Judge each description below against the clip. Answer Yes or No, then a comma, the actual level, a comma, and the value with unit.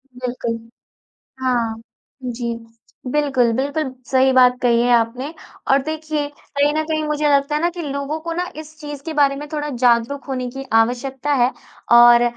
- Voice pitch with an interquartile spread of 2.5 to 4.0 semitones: Yes, average, 3.2 semitones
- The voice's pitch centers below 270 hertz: No, very high, 275 Hz